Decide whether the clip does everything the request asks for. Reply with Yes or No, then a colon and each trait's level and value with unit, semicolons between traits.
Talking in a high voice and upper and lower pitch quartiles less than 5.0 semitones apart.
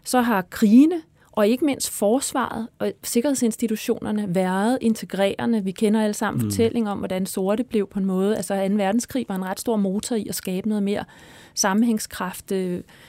Yes: high, 210 Hz; average, 2.9 semitones